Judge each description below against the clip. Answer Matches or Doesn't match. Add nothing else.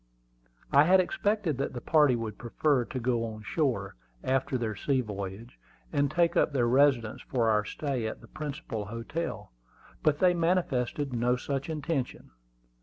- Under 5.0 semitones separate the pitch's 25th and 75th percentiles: Matches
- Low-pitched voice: Matches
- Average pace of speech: Matches